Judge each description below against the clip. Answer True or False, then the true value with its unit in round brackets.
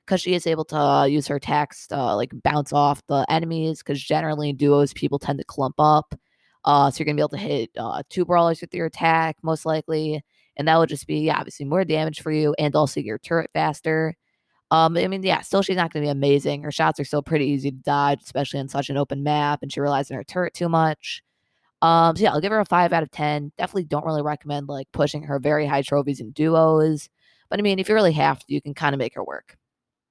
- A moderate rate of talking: False (255 wpm)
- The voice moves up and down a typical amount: False (2.1 semitones)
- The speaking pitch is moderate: True (150 Hz)